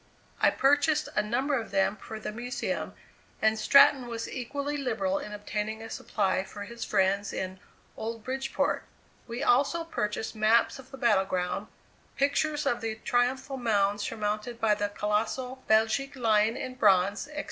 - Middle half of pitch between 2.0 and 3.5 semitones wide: No, average, 4.1 semitones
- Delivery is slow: No, average, 160 wpm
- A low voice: No, high, 225 Hz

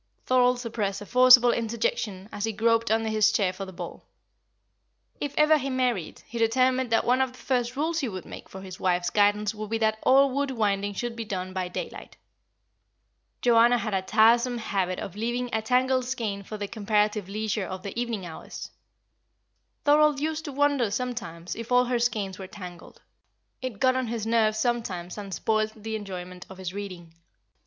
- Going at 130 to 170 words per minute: No, average, 185 wpm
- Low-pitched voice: No, high, 220 Hz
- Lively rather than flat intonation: No, average, 4.0 semitones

